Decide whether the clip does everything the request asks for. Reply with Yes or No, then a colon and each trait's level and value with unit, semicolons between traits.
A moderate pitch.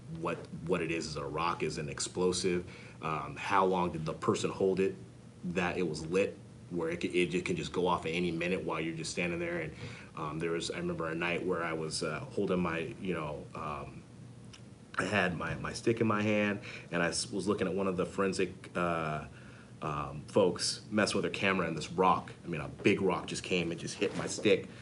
No: very low, 90 Hz